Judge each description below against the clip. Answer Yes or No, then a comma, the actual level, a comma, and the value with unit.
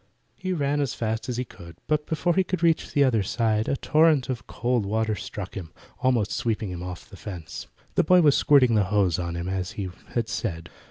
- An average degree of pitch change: No, wide, 6.7 semitones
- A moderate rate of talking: No, fast, 220 wpm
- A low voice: Yes, low, 115 Hz